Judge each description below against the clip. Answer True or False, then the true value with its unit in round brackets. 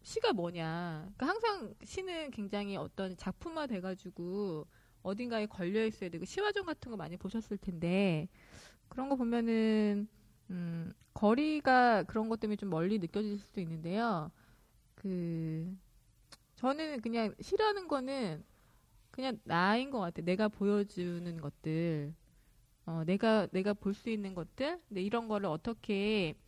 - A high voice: True (205 Hz)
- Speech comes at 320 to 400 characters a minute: False (275 characters per minute)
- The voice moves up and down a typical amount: True (5.0 semitones)